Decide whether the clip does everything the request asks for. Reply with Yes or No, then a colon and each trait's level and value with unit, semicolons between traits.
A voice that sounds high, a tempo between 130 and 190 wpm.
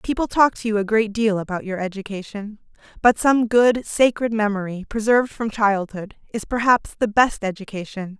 Yes: high, 215 Hz; average, 170 wpm